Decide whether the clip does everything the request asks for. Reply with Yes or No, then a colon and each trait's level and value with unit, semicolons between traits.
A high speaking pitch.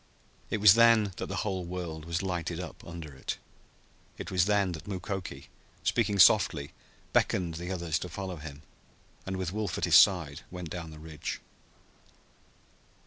No: very low, 90 Hz